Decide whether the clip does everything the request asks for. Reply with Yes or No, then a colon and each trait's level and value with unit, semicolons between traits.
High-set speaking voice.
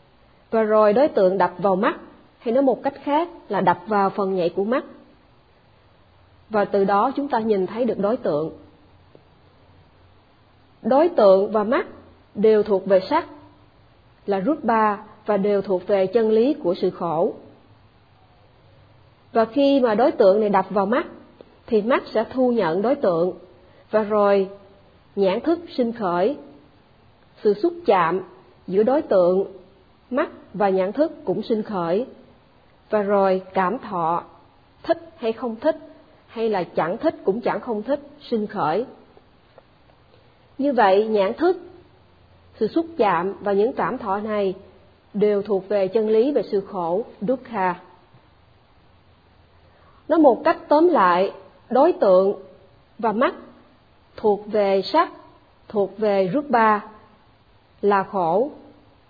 Yes: high, 210 Hz